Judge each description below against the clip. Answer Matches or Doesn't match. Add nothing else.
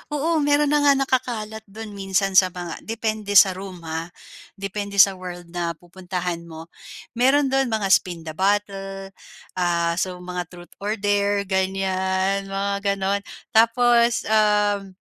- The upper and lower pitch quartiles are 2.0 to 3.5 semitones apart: Matches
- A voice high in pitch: Matches